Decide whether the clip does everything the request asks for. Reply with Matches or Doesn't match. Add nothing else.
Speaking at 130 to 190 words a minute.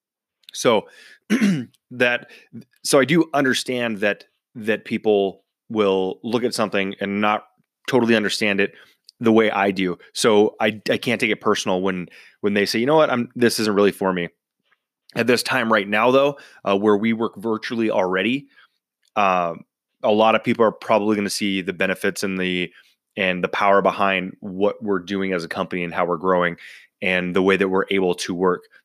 Matches